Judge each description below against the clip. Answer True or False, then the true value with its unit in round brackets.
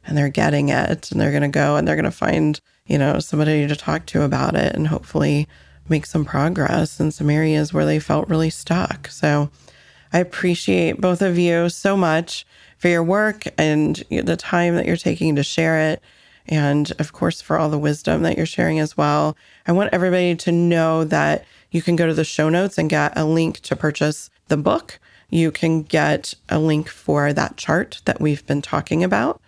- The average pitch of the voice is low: False (155 Hz)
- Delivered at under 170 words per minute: False (205 wpm)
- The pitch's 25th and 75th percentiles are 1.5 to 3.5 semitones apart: True (2.8 semitones)